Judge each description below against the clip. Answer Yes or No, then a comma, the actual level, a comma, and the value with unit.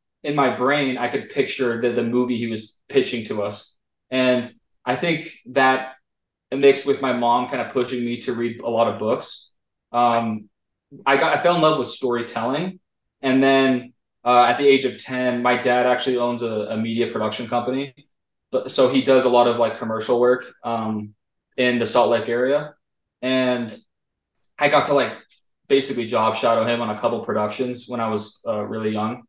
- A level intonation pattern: Yes, narrow, 2.0 semitones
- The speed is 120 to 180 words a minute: No, average, 190 wpm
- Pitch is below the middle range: Yes, low, 125 Hz